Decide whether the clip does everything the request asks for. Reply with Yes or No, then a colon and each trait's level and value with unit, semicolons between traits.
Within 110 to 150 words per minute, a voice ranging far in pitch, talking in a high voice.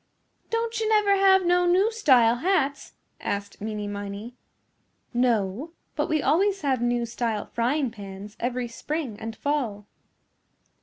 Yes: slow, 135 wpm; wide, 8.2 semitones; very high, 250 Hz